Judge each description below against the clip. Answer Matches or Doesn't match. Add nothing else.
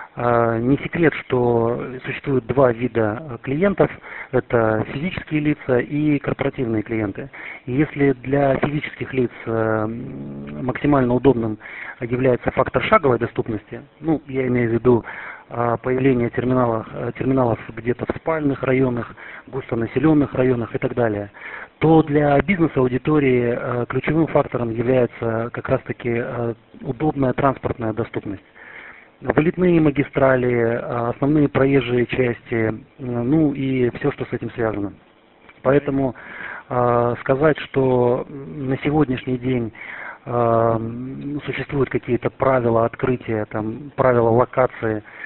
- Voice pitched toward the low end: Matches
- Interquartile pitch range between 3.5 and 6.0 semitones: Doesn't match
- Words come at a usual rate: Doesn't match